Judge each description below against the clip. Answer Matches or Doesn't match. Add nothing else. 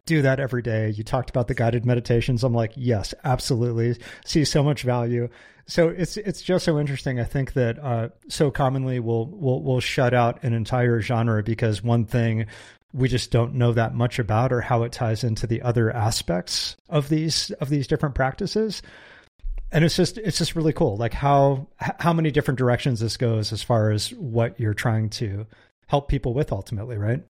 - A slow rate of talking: Doesn't match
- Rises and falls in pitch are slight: Doesn't match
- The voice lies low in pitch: Matches